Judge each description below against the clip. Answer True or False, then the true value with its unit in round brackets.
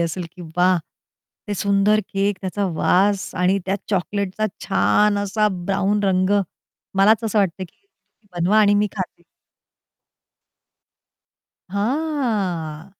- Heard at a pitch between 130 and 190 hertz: False (200 Hz)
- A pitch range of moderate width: False (2.1 semitones)